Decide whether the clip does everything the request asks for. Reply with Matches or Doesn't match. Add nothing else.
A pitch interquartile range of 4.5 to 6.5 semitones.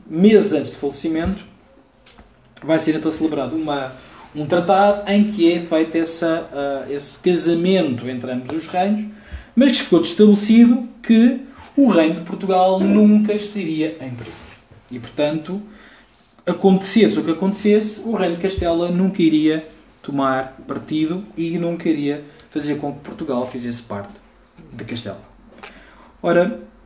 Matches